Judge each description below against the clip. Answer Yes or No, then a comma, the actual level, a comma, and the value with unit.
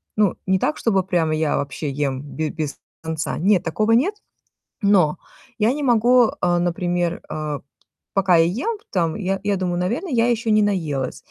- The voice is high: No, medium, 180 Hz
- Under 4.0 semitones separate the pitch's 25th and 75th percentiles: No, average, 5.1 semitones